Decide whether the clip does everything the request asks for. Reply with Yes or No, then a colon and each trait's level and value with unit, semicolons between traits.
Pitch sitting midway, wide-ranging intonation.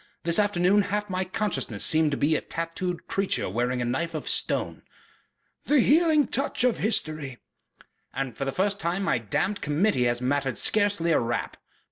Yes: medium, 170 Hz; wide, 7.1 semitones